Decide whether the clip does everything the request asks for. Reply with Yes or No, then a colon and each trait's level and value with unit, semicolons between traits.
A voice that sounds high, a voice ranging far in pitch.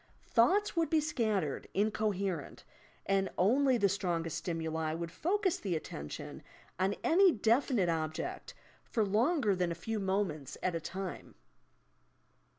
Yes: high, 195 Hz; wide, 5.9 semitones